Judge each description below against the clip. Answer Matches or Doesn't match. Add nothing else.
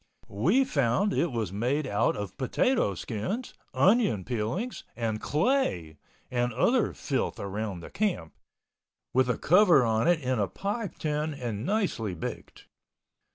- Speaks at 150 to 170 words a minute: Doesn't match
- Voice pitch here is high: Doesn't match